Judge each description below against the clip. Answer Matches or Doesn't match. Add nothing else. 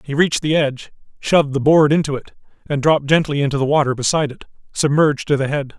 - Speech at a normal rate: Doesn't match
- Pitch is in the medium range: Matches